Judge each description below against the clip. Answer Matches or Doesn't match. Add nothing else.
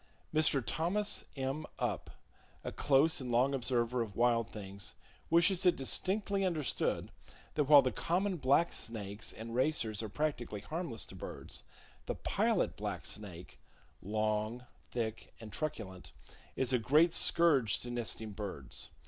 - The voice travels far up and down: Matches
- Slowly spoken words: Matches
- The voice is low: Matches